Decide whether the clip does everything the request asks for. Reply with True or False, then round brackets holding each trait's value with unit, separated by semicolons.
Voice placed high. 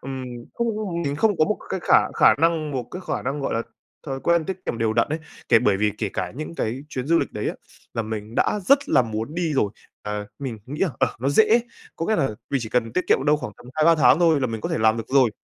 False (135 Hz)